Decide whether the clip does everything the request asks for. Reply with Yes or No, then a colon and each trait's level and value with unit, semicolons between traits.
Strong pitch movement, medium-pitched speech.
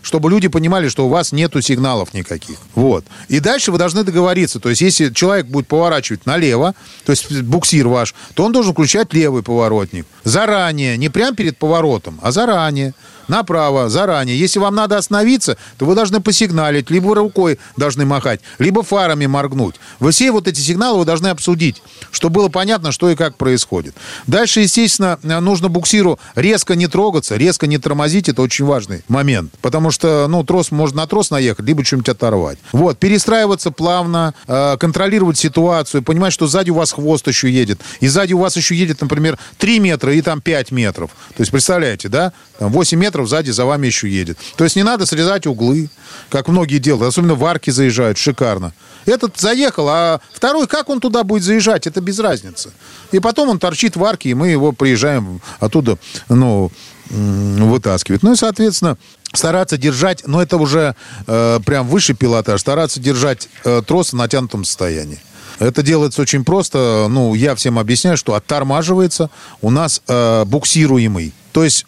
Yes: wide, 6.2 semitones; medium, 150 Hz